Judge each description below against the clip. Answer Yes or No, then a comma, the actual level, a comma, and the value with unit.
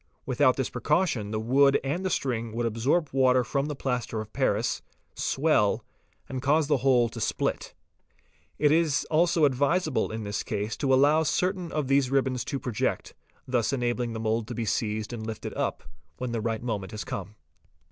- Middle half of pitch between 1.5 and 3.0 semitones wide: No, average, 4.0 semitones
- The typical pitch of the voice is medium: No, low, 125 Hz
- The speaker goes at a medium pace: Yes, average, 180 wpm